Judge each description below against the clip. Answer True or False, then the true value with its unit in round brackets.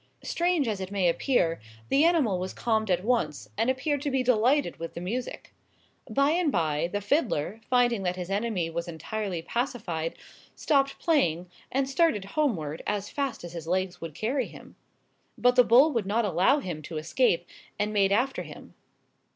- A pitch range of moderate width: False (7.0 semitones)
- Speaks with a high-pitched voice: True (210 Hz)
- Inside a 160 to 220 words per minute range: True (175 wpm)